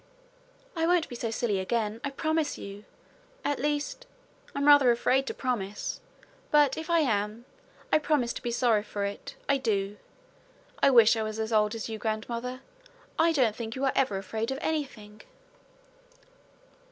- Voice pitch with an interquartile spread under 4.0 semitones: No, average, 4.7 semitones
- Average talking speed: Yes, average, 165 wpm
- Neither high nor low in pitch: No, high, 235 Hz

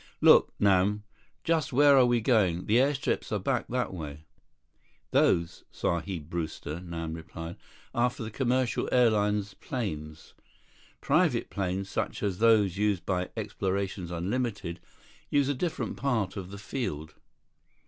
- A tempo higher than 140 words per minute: No, slow, 135 wpm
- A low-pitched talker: Yes, low, 100 Hz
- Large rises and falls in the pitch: Yes, wide, 5.9 semitones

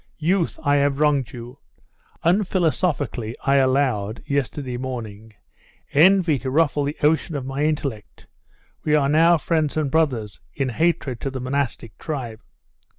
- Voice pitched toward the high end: No, medium, 140 Hz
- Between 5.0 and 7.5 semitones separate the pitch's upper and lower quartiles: No, average, 3.7 semitones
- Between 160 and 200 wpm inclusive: No, average, 140 wpm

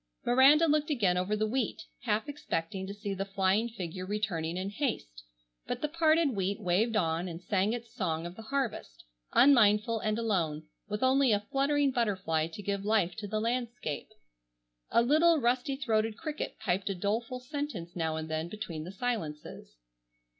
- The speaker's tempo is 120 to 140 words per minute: No, average, 170 wpm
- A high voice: Yes, high, 210 Hz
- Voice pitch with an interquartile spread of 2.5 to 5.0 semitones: No, wide, 5.5 semitones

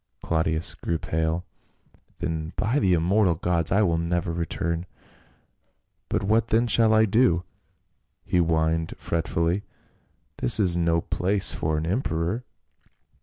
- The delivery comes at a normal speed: No, slow, 125 wpm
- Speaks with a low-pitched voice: Yes, very low, 85 Hz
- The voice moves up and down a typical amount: Yes, average, 3.3 semitones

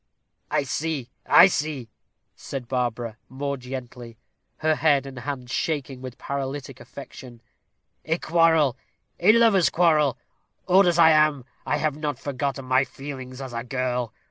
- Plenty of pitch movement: No, average, 3.4 semitones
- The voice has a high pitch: No, medium, 140 Hz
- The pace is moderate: Yes, average, 145 wpm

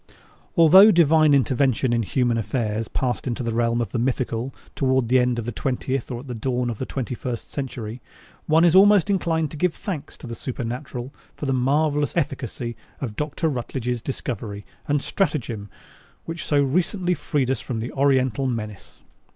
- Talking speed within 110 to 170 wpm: No, average, 180 wpm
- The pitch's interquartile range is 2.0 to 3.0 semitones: No, average, 3.8 semitones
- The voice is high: No, low, 130 Hz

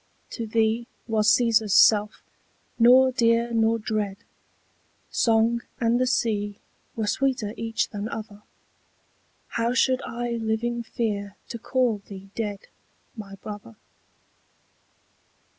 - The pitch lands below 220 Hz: No, high, 225 Hz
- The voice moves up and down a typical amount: No, narrow, 2.1 semitones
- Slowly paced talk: Yes, slow, 110 wpm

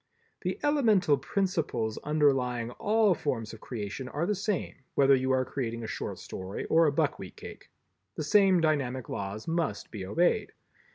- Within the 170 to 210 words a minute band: No, average, 160 wpm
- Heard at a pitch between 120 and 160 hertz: Yes, medium, 140 Hz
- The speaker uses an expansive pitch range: Yes, wide, 7.0 semitones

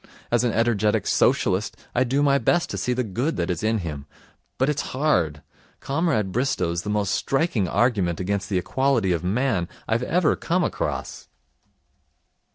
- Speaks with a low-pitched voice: Yes, low, 115 Hz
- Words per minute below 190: Yes, average, 165 wpm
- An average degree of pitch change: No, wide, 6.6 semitones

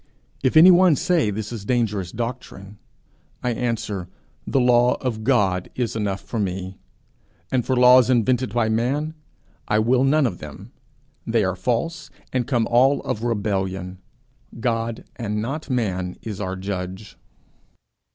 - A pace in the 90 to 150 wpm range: Yes, average, 145 wpm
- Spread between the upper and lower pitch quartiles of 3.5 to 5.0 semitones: Yes, average, 4.2 semitones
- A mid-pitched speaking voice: No, low, 115 Hz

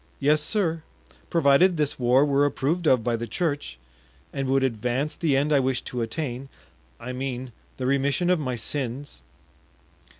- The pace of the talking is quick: No, average, 155 wpm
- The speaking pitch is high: No, low, 135 Hz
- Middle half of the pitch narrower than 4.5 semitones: Yes, average, 3.2 semitones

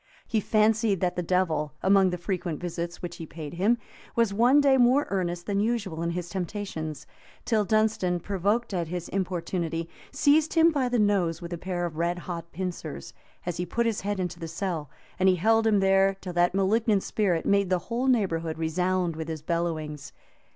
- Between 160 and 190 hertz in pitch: Yes, medium, 185 Hz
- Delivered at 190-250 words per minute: Yes, average, 195 wpm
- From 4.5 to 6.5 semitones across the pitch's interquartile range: No, average, 3.8 semitones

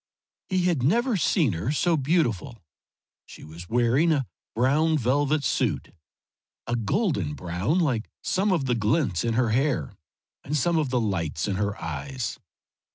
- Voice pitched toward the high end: No, low, 130 Hz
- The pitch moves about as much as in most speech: No, wide, 7.1 semitones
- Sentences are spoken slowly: No, average, 155 wpm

